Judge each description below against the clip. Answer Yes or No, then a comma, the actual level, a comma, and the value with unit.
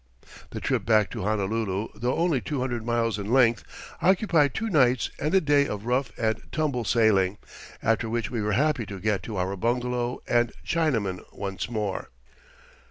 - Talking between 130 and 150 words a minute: No, average, 170 wpm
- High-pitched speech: No, low, 115 Hz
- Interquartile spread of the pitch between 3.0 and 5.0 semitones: Yes, average, 3.9 semitones